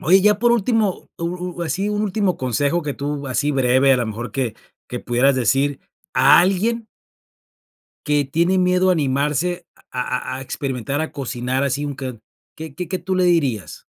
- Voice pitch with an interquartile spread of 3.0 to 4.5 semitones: No, wide, 5.4 semitones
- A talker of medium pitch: Yes, medium, 145 Hz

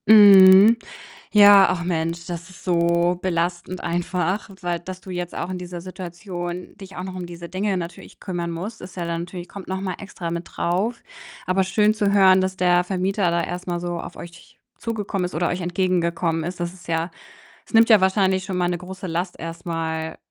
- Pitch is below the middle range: No, medium, 180 Hz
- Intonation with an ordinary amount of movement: No, narrow, 1.7 semitones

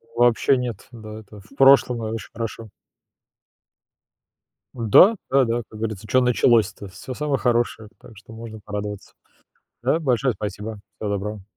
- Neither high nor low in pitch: No, low, 115 Hz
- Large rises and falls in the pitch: No, average, 2.7 semitones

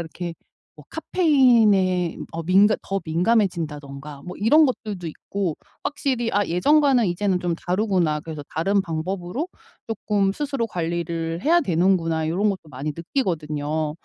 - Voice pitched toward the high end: No, medium, 180 Hz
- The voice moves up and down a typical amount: Yes, average, 4.8 semitones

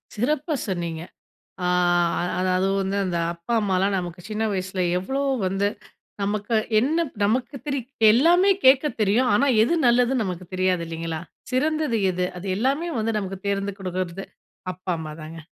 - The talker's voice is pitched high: Yes, high, 200 Hz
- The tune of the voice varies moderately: No, wide, 5.8 semitones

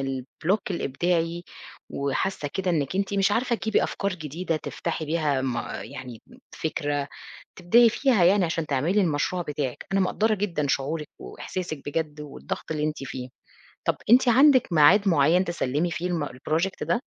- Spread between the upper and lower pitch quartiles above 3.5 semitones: Yes, average, 4.8 semitones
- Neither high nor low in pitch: Yes, medium, 165 Hz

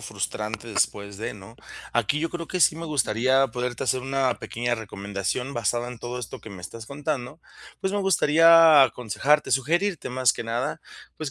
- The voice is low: Yes, low, 125 Hz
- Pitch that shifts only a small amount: No, average, 4.8 semitones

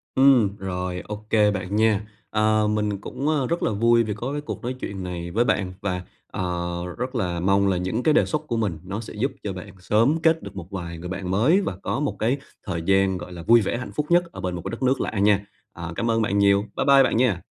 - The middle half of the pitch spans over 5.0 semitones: No, average, 4.4 semitones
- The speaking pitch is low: Yes, low, 105 Hz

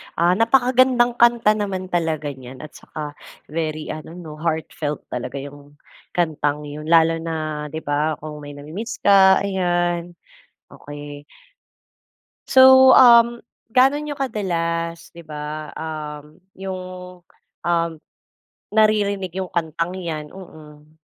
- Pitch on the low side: No, medium, 165 Hz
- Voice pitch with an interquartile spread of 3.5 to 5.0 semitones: Yes, average, 4.4 semitones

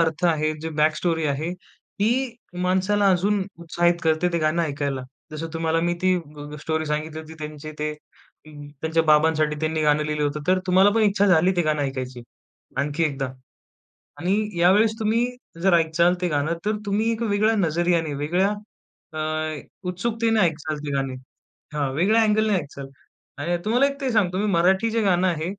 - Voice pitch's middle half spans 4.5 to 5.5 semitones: No, average, 4.0 semitones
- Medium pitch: Yes, medium, 165 Hz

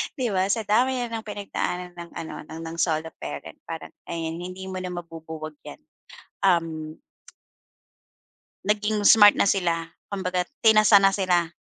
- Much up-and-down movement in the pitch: No, average, 3.9 semitones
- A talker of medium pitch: Yes, medium, 180 Hz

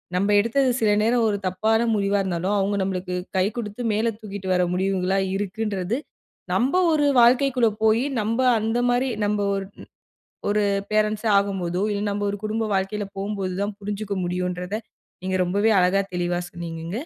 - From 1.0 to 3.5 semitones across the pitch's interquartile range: Yes, average, 2.8 semitones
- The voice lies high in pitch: Yes, high, 205 Hz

